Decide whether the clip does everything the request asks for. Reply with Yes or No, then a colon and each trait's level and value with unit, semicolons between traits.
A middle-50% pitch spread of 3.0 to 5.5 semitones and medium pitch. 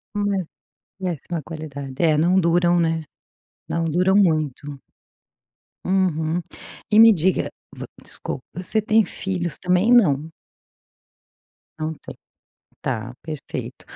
Yes: average, 3.5 semitones; medium, 170 Hz